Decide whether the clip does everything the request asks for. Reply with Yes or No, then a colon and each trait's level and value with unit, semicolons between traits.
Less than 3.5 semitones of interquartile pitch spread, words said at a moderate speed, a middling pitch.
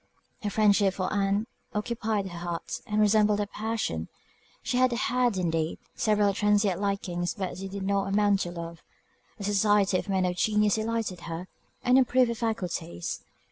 No: average, 2.7 semitones; average, 165 wpm; high, 200 Hz